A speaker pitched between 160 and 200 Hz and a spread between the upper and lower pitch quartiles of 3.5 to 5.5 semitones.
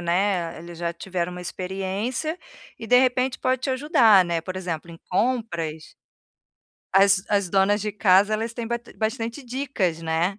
Yes: high, 195 Hz; average, 5.2 semitones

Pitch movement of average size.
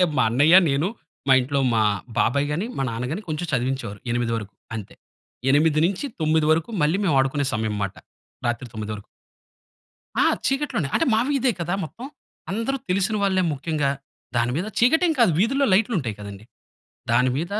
No: wide, 7.9 semitones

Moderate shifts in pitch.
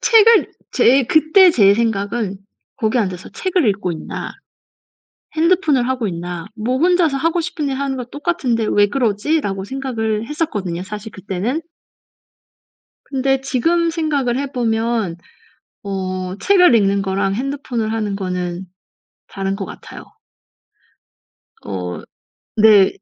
No: wide, 6.5 semitones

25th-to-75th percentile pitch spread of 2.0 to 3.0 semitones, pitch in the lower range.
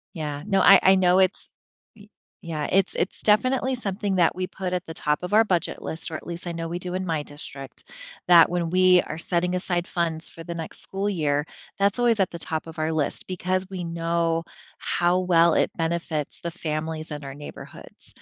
No: narrow, 2.4 semitones; medium, 175 Hz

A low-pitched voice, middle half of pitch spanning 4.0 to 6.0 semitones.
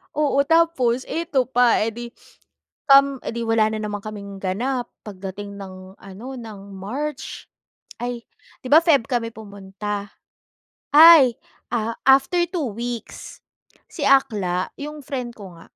No: high, 235 Hz; average, 5.1 semitones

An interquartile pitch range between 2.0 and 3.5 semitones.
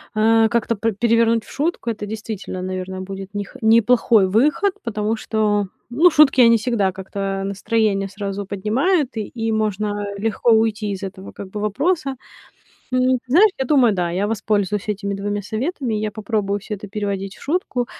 Yes: average, 2.8 semitones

